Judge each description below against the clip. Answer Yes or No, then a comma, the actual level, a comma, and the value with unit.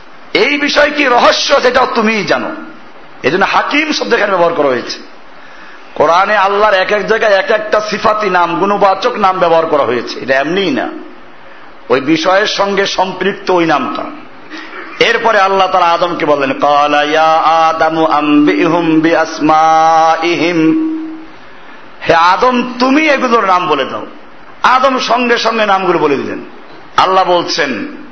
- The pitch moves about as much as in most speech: No, wide, 7.3 semitones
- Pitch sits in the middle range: No, high, 195 Hz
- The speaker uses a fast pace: Yes, fast, 130 wpm